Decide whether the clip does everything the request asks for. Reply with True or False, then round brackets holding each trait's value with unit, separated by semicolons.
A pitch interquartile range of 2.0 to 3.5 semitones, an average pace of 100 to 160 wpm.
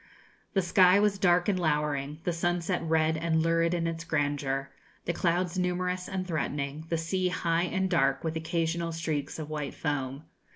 False (2.7 semitones; 170 wpm)